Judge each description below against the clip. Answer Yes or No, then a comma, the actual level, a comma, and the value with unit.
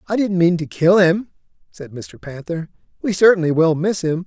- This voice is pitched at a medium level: Yes, medium, 170 Hz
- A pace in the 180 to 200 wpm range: Yes, average, 195 wpm